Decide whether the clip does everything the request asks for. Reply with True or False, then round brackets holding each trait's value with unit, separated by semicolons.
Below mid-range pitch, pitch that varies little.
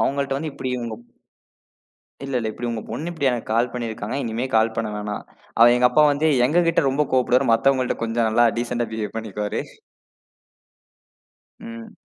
False (120 Hz; 3.3 semitones)